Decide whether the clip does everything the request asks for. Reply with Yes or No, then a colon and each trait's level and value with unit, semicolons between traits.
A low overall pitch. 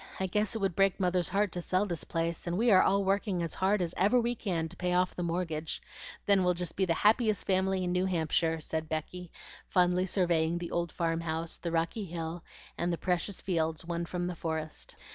No: medium, 180 Hz